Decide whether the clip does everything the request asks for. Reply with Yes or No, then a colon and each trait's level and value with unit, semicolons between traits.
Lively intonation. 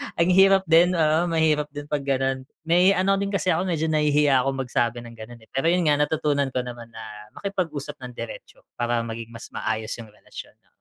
Yes: wide, 5.7 semitones